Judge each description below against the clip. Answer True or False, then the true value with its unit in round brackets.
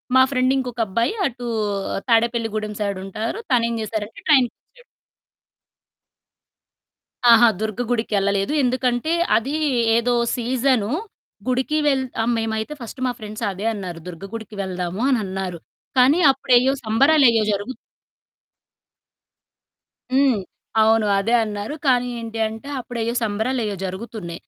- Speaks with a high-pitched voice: True (230 Hz)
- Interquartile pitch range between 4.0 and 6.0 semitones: False (3.3 semitones)